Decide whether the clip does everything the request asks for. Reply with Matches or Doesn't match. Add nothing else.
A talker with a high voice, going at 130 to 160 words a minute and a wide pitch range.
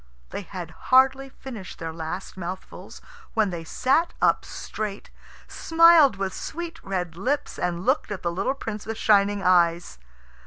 Matches